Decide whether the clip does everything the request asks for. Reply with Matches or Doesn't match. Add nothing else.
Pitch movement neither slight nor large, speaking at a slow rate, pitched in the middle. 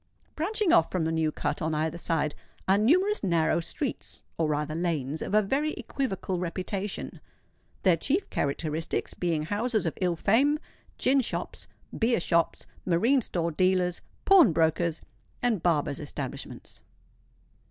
Doesn't match